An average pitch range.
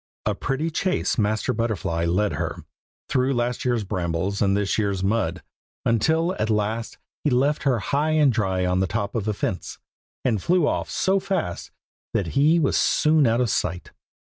No: wide, 6.3 semitones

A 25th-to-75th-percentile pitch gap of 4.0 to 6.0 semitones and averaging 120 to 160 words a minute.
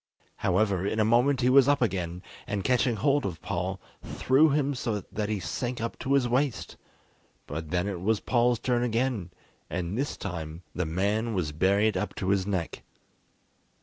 No: average, 5.1 semitones; average, 180 wpm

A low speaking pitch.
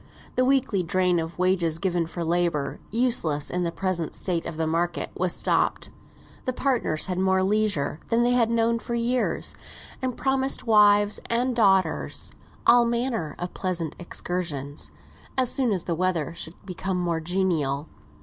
No: medium, 185 Hz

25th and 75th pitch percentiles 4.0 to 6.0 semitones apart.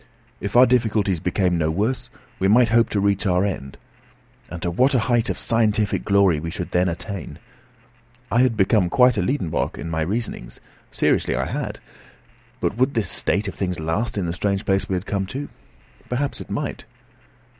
Yes: average, 4.4 semitones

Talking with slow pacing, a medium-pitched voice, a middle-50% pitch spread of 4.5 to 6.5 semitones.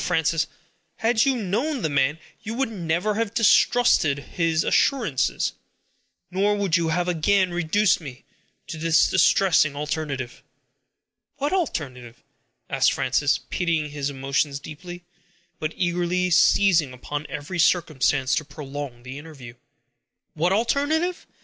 Yes: slow, 125 wpm; medium, 165 Hz; wide, 5.6 semitones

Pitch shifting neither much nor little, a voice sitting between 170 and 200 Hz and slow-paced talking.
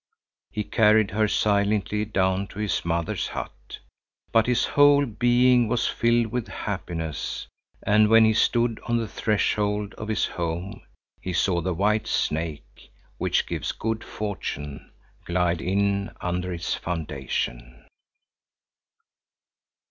No: average, 4.1 semitones; low, 100 Hz; slow, 125 wpm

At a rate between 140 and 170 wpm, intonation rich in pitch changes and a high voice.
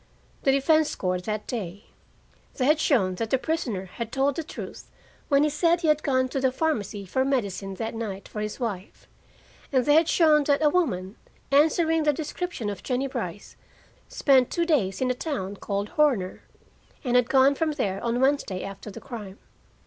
No: average, 185 wpm; wide, 6.5 semitones; very high, 260 Hz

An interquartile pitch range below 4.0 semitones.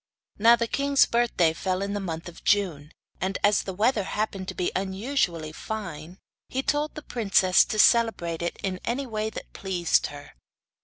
No: average, 4.8 semitones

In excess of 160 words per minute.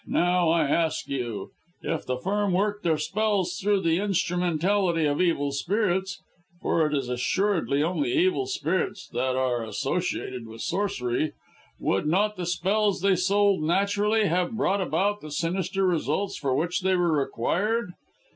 No: average, 150 wpm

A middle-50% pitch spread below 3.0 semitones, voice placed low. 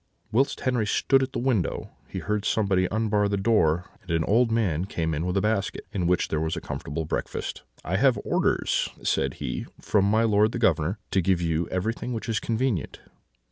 No: average, 4.7 semitones; low, 100 Hz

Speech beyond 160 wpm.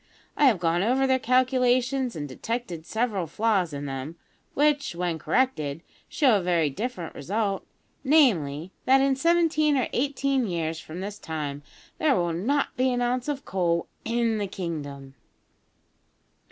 No: average, 150 wpm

